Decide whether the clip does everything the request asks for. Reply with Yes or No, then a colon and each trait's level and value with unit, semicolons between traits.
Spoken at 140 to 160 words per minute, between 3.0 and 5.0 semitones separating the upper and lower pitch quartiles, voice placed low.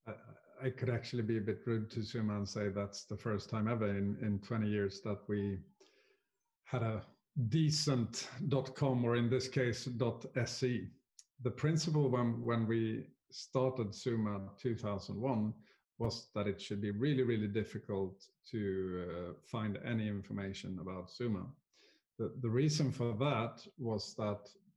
Yes: average, 150 wpm; average, 3.8 semitones; low, 115 Hz